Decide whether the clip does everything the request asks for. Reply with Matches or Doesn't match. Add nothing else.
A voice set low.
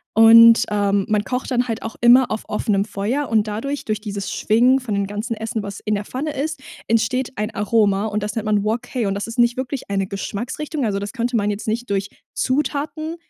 Doesn't match